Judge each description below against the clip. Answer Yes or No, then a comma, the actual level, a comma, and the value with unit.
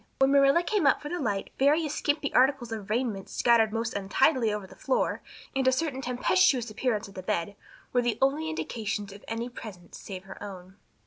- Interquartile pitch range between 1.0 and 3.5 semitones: No, average, 5.1 semitones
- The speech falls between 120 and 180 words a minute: No, average, 195 wpm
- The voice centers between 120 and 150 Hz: No, high, 240 Hz